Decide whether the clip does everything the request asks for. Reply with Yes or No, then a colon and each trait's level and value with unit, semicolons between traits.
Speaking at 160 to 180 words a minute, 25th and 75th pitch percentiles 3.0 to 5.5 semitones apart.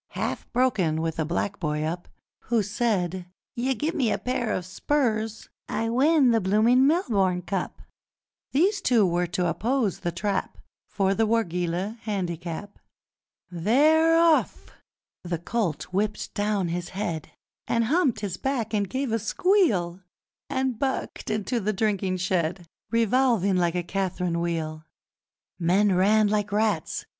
No: slow, 135 wpm; average, 5.0 semitones